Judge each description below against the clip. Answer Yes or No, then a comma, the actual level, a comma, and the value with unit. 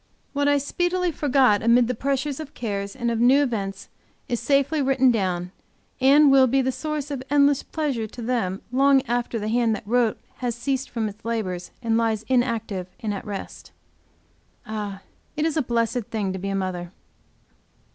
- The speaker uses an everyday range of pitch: Yes, average, 4.3 semitones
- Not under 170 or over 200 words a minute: Yes, average, 180 wpm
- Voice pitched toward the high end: Yes, high, 240 Hz